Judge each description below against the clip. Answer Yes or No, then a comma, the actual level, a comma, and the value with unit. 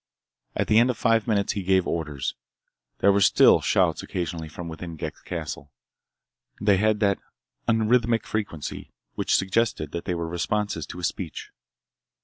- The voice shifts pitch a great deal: No, average, 4.5 semitones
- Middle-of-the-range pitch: No, very low, 95 Hz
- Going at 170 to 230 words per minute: No, average, 155 wpm